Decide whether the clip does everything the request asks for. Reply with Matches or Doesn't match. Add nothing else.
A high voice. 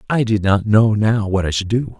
Doesn't match